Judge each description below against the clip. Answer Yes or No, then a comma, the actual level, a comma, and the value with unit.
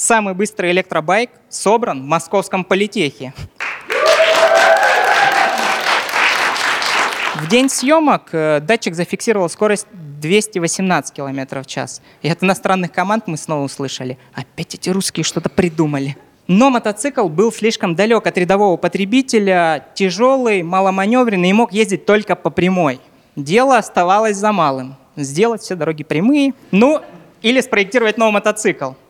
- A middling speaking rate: Yes, average, 120 wpm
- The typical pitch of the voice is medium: No, high, 195 Hz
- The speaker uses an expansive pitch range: Yes, wide, 5.7 semitones